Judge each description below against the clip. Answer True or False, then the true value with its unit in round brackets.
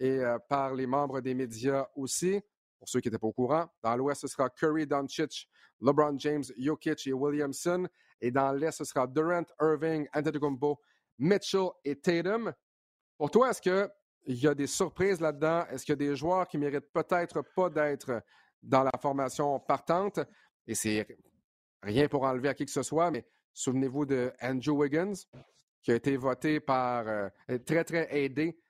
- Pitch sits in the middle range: True (145 Hz)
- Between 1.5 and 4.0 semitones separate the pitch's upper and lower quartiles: True (3.5 semitones)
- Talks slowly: False (180 wpm)